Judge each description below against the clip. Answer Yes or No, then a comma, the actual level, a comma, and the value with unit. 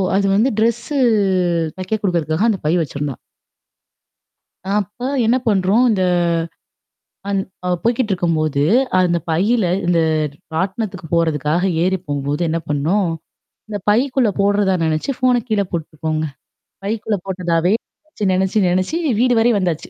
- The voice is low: No, high, 190 Hz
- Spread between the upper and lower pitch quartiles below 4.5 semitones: No, average, 4.8 semitones